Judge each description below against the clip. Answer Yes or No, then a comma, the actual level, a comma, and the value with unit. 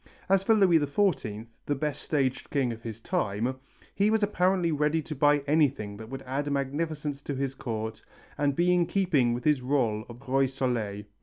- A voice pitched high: No, medium, 140 Hz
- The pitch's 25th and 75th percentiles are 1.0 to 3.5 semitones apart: No, average, 4.2 semitones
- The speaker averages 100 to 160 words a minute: No, average, 185 wpm